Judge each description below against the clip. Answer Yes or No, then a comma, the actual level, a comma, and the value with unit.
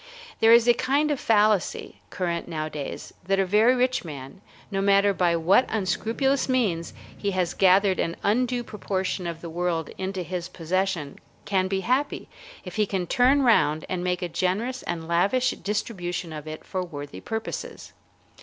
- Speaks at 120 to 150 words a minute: No, average, 165 wpm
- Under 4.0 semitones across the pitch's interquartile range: No, average, 4.5 semitones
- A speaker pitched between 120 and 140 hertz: No, high, 190 Hz